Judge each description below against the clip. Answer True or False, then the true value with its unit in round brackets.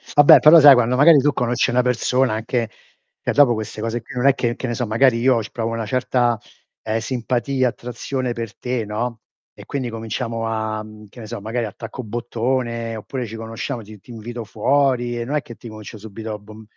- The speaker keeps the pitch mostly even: True (2.2 semitones)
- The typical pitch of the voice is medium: False (120 Hz)